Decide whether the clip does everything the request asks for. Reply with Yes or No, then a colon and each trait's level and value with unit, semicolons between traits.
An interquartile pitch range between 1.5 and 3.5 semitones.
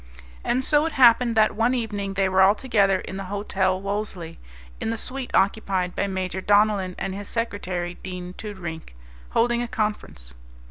Yes: average, 3.2 semitones